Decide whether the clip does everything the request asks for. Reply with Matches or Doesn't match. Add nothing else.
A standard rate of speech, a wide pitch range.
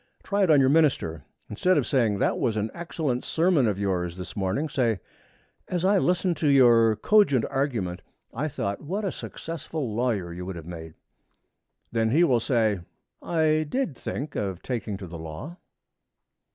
Matches